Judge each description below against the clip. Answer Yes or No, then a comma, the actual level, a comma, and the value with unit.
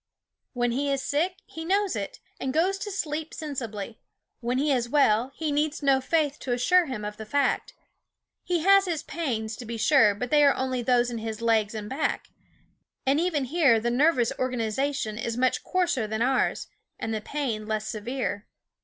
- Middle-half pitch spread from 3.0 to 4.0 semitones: No, average, 5.0 semitones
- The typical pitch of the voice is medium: No, very high, 260 Hz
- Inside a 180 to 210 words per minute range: Yes, average, 190 wpm